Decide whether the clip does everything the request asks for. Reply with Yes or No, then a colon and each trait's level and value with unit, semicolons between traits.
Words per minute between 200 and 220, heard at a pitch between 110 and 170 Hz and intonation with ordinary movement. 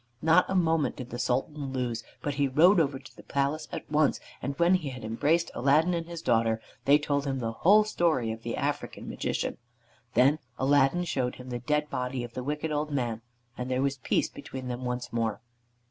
Yes: fast, 205 wpm; medium, 140 Hz; average, 3.7 semitones